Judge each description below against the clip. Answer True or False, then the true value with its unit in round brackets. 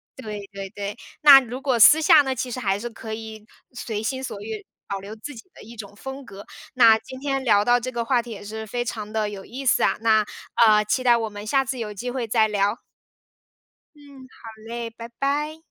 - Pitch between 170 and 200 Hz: False (230 Hz)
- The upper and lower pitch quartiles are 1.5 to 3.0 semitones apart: False (3.5 semitones)